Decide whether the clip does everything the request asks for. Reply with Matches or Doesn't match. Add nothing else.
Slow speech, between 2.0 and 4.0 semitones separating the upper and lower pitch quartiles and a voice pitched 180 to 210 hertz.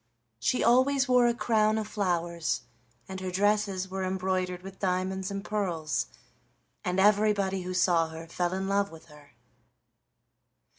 Doesn't match